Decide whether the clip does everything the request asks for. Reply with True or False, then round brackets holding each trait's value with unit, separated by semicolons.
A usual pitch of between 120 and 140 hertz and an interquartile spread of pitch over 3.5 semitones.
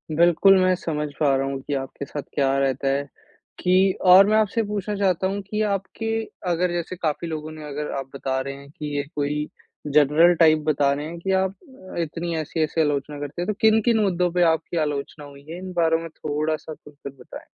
False (155 Hz; 4.0 semitones)